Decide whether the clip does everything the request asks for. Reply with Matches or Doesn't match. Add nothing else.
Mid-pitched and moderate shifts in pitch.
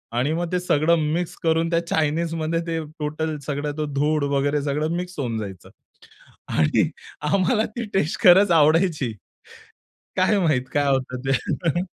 Matches